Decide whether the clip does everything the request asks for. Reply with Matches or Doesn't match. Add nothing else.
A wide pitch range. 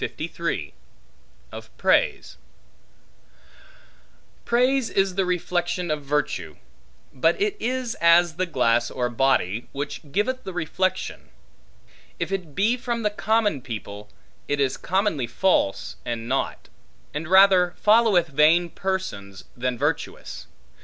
Matches